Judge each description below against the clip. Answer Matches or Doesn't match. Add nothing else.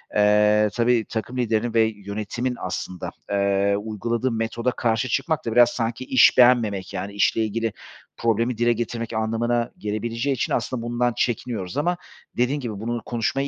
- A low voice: Matches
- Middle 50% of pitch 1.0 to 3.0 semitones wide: Matches